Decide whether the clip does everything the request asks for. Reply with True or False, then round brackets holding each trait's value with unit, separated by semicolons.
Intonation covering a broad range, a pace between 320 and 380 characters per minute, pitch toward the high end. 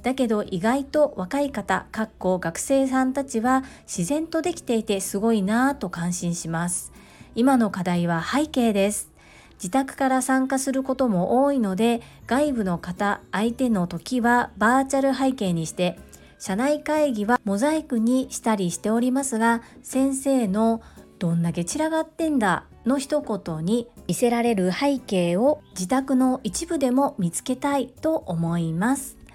False (5.8 semitones; 305 characters per minute; 240 Hz)